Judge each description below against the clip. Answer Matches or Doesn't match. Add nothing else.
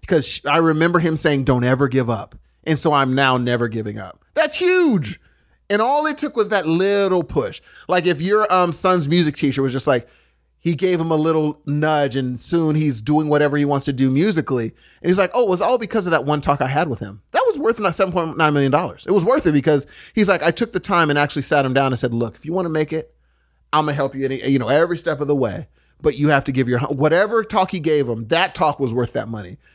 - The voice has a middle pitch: Matches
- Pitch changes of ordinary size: Matches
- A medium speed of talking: Doesn't match